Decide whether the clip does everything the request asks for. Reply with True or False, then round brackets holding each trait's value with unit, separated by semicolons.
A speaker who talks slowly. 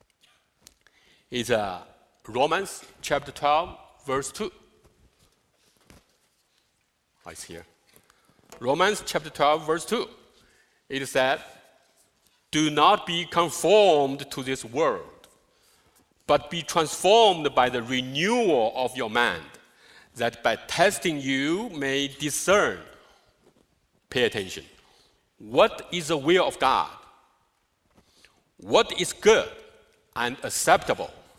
True (100 wpm)